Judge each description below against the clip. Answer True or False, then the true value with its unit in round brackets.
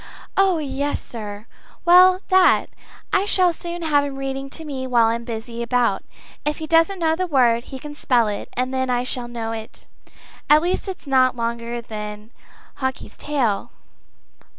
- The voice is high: True (260 Hz)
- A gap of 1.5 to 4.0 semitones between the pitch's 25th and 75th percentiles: False (5.2 semitones)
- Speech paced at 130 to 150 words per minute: False (175 wpm)